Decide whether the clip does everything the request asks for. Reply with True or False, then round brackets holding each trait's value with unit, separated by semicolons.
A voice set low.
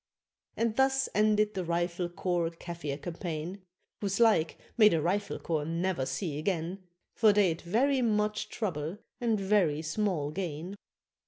False (185 Hz)